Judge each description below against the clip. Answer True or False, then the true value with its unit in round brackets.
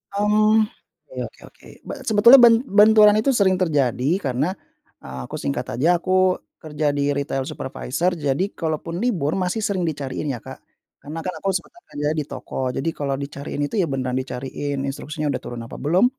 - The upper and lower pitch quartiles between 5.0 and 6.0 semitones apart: True (5.4 semitones)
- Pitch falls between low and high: True (155 Hz)